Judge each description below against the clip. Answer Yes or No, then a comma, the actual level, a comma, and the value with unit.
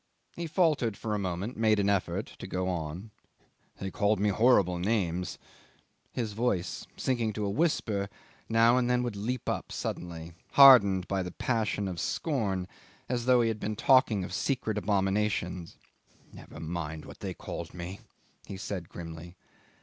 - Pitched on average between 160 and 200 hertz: No, low, 100 Hz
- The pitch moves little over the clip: No, average, 4.3 semitones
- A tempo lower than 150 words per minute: No, average, 165 wpm